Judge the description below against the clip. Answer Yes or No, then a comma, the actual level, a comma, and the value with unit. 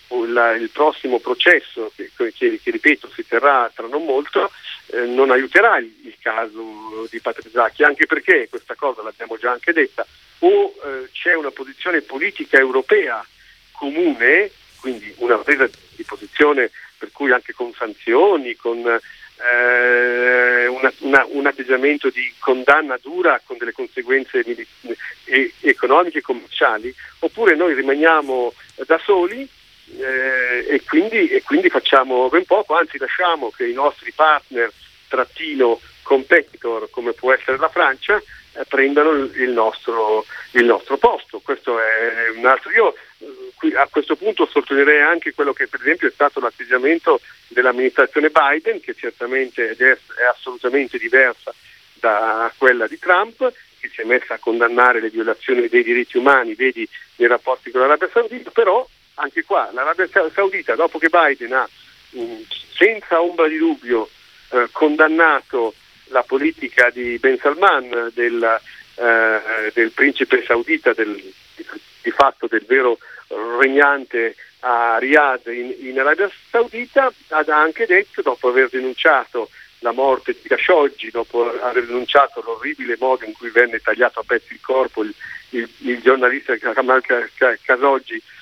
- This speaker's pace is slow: No, average, 145 wpm